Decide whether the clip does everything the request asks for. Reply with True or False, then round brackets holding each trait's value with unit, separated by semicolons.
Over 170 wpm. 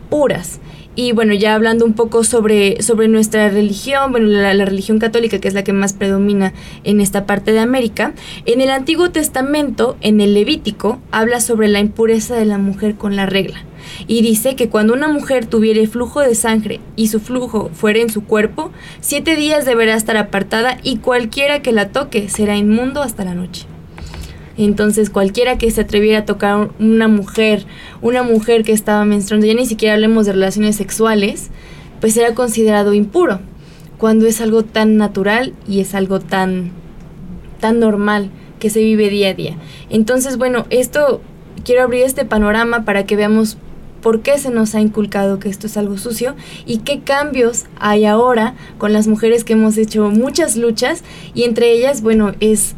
True (180 wpm)